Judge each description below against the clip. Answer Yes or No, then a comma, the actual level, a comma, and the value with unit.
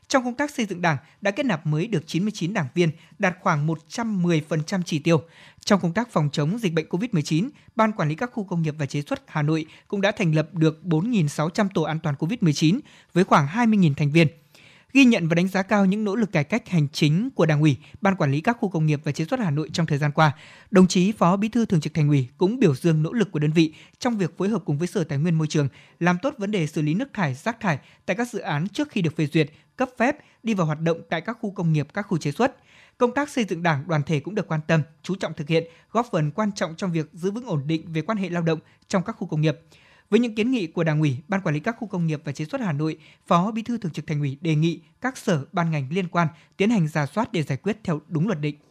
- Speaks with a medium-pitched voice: Yes, medium, 170 Hz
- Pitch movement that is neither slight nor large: Yes, average, 4.6 semitones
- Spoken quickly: Yes, fast, 280 wpm